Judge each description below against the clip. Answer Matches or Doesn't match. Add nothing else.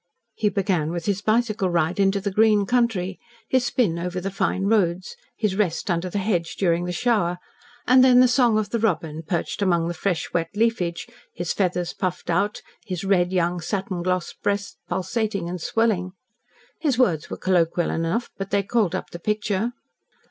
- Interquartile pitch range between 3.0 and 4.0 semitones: Matches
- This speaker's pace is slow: Doesn't match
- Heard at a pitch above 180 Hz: Matches